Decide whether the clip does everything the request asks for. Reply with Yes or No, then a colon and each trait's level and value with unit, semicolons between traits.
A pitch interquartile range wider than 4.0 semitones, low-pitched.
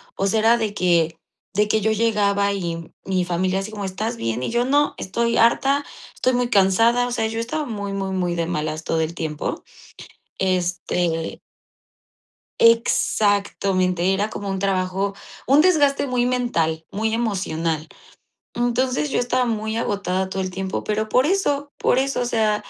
No: average, 4.4 semitones; high, 205 Hz